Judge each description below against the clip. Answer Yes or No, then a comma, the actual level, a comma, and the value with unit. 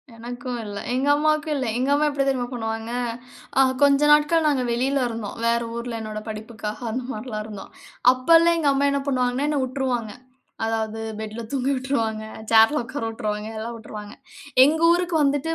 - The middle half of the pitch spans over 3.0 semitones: Yes, average, 4.1 semitones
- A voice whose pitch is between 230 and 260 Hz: Yes, very high, 250 Hz